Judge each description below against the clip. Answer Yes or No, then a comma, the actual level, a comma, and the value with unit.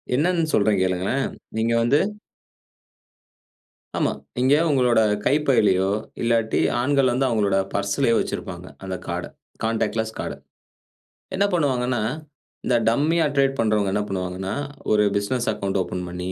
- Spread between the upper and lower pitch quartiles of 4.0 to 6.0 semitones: Yes, average, 5.1 semitones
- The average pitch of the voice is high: No, low, 115 Hz